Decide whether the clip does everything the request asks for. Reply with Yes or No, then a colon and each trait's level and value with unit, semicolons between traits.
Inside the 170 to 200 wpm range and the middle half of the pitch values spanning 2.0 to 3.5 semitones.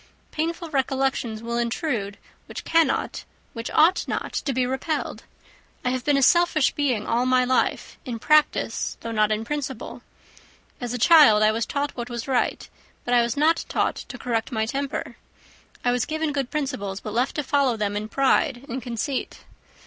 No: average, 180 wpm; average, 3.9 semitones